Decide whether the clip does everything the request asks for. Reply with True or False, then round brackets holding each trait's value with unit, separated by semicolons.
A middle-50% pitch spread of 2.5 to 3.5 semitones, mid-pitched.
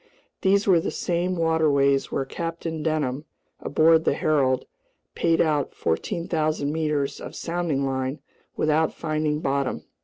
True (2.9 semitones; 155 Hz)